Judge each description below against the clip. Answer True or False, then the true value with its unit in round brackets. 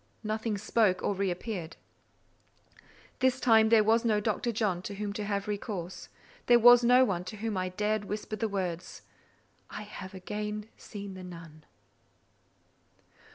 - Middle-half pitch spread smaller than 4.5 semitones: True (2.8 semitones)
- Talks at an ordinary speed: True (155 wpm)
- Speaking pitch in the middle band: False (210 Hz)